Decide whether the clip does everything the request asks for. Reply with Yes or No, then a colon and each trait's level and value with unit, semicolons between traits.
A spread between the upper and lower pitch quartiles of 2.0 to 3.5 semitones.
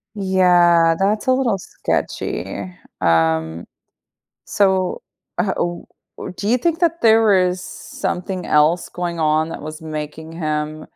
No: average, 4.1 semitones